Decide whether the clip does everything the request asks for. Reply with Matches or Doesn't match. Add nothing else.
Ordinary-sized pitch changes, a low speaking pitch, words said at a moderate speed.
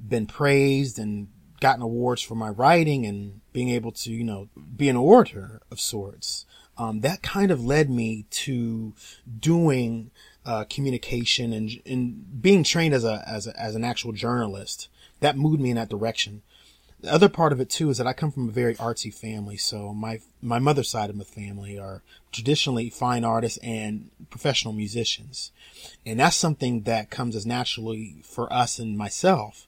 Matches